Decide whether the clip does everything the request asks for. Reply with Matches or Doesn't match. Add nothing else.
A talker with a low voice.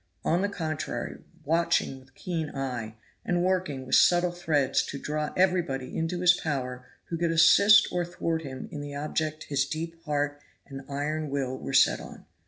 Doesn't match